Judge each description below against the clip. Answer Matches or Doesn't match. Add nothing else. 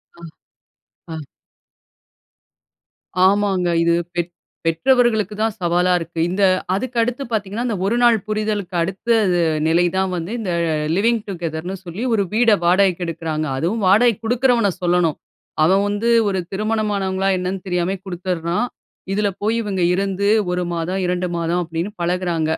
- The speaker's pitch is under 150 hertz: Doesn't match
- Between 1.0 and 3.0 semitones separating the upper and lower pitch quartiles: Doesn't match